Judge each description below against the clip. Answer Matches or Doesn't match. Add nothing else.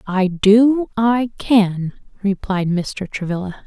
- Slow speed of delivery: Matches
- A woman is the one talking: Matches